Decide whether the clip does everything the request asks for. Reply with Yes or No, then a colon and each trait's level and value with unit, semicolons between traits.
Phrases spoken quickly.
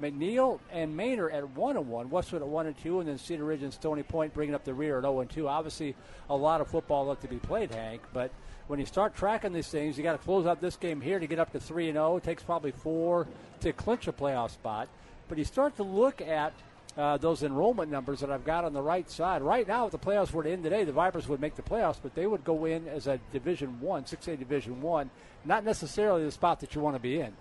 Yes: fast, 250 wpm